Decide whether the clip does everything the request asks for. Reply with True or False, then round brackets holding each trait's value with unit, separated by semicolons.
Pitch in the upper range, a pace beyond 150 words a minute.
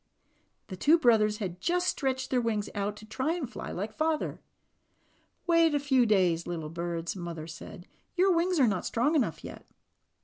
True (230 Hz; 175 wpm)